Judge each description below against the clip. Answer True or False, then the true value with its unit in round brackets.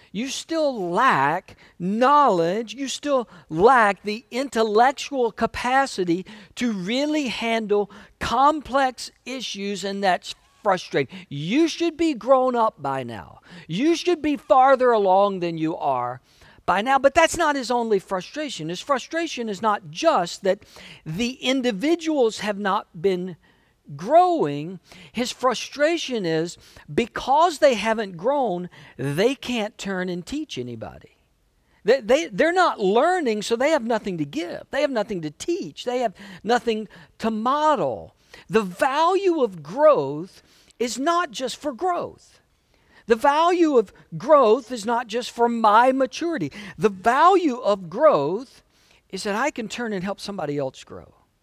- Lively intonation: True (6.7 semitones)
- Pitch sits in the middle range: False (230 Hz)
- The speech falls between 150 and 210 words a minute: False (140 wpm)